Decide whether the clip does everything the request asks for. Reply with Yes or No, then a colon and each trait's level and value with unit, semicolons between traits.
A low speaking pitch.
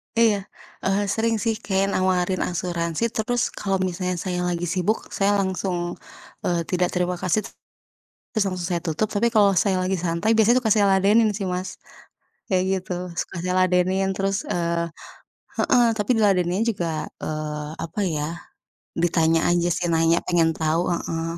No: medium, 185 Hz